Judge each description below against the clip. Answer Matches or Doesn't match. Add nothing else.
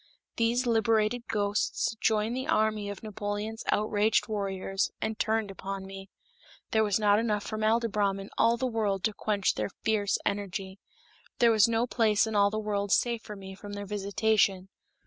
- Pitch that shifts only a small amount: Matches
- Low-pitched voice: Doesn't match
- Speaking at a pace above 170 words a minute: Doesn't match